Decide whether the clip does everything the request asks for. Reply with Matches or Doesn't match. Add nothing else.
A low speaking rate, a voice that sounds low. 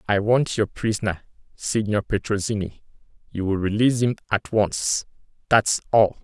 Matches